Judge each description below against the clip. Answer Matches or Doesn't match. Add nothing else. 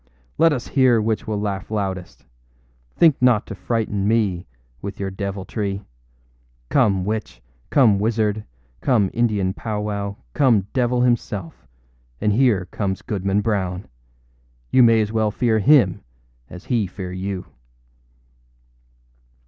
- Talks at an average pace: Doesn't match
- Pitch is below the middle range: Matches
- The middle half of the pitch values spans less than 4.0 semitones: Matches